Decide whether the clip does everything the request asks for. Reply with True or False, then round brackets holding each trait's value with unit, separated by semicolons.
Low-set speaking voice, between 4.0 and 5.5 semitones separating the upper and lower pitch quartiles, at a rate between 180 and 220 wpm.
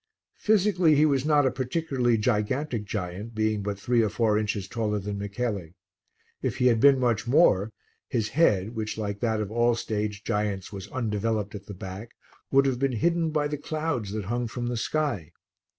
True (115 Hz; 4.5 semitones; 185 wpm)